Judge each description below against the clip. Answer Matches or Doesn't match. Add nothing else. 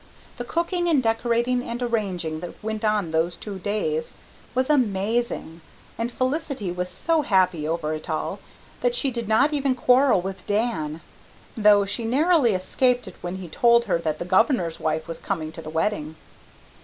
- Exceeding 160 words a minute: Matches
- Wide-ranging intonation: Matches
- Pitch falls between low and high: Doesn't match